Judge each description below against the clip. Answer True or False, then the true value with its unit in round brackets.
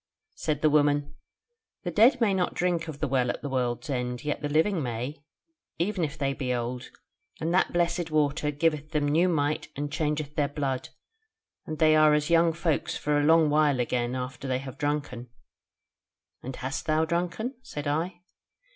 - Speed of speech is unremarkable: True (180 wpm)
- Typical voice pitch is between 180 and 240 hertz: False (150 Hz)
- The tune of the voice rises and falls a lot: False (3.1 semitones)